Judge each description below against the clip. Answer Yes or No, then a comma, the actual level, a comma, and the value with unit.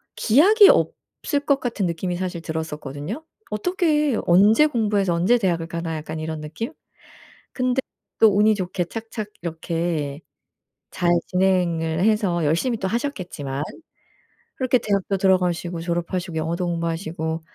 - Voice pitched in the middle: Yes, medium, 180 Hz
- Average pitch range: Yes, average, 5.0 semitones